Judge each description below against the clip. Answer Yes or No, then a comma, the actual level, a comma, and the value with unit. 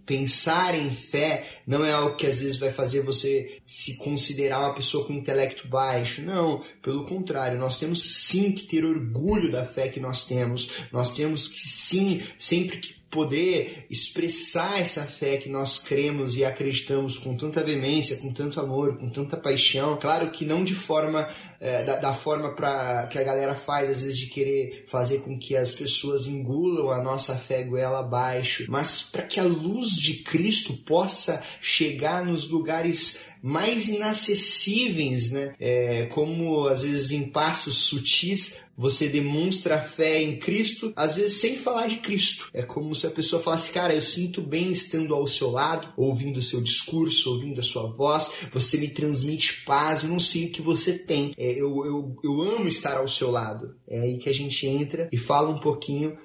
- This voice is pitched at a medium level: Yes, medium, 145 Hz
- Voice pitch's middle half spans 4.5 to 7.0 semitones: No, average, 3.4 semitones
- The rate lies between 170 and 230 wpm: Yes, average, 180 wpm